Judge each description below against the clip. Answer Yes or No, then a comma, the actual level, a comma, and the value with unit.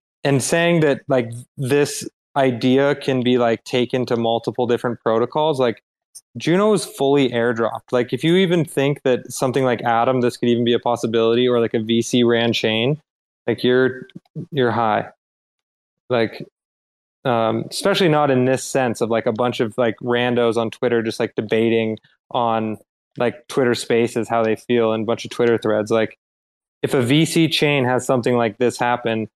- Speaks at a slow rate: No, average, 175 wpm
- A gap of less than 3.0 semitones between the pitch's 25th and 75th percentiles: Yes, narrow, 2.6 semitones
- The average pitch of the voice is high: No, low, 120 Hz